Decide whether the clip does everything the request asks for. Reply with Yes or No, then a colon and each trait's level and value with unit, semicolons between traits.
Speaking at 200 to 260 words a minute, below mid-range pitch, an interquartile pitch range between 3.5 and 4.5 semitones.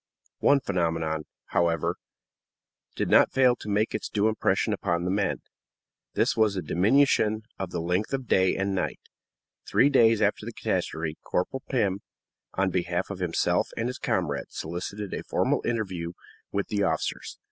No: average, 160 wpm; very low, 95 Hz; average, 4.0 semitones